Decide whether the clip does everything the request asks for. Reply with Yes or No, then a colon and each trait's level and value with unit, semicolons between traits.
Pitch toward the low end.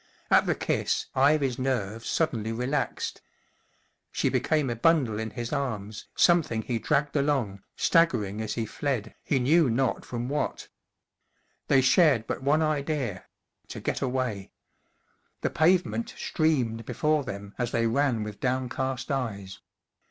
Yes: low, 130 Hz